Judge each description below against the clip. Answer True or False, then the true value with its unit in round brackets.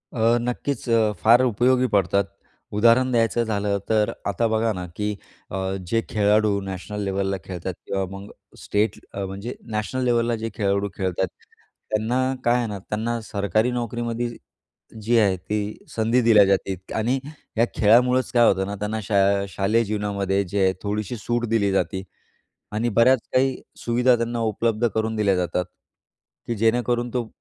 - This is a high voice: False (110 Hz)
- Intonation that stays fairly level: False (3.0 semitones)